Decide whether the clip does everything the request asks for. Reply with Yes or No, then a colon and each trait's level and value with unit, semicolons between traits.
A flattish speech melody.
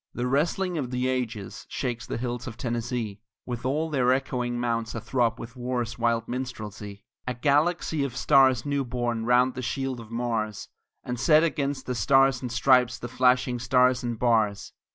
Yes: narrow, 1.9 semitones